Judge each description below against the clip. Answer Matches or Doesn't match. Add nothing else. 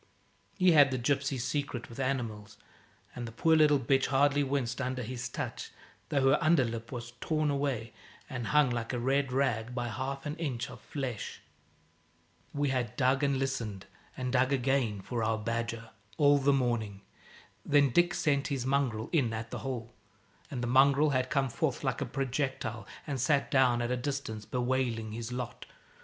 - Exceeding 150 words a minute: Matches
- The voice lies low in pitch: Matches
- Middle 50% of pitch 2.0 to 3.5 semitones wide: Matches